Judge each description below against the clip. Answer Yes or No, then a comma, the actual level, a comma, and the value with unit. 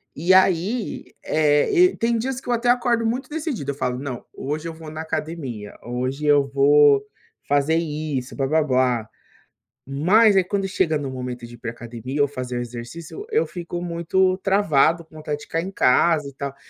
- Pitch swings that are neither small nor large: No, wide, 5.7 semitones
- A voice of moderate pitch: Yes, medium, 155 Hz